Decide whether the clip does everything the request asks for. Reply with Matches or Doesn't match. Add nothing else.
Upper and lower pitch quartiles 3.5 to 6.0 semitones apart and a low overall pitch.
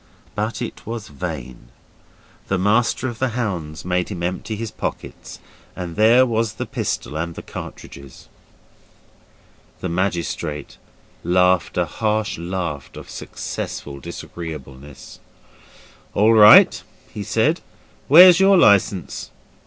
Matches